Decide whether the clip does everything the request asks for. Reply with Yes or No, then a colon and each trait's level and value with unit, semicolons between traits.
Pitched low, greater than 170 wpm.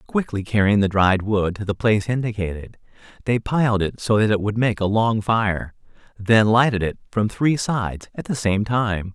Yes: low, 105 Hz; average, 195 wpm